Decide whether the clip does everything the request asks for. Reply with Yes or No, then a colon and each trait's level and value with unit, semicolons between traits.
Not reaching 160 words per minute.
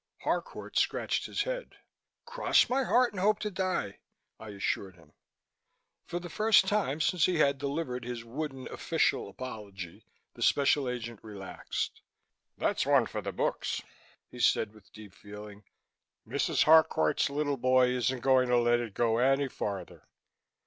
Yes: average, 150 wpm